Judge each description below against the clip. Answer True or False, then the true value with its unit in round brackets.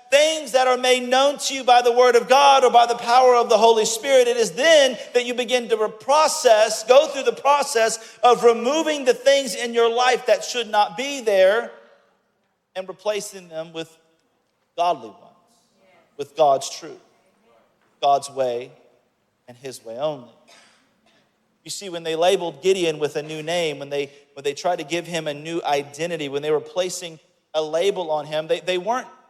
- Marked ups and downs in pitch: True (7.6 semitones)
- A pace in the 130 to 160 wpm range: False (185 wpm)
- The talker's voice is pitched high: True (200 Hz)